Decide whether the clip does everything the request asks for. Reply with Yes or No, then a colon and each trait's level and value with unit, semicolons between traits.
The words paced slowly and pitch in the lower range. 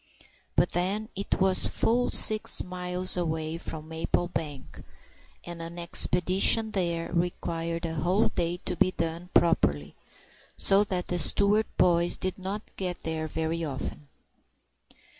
No: slow, 130 wpm; medium, 175 Hz